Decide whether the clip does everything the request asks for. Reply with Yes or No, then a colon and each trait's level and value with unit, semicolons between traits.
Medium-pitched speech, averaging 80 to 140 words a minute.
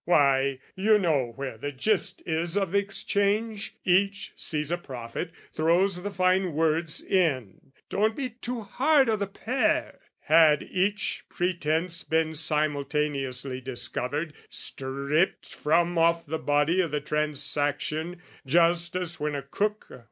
Yes: medium, 165 Hz; slow, 135 wpm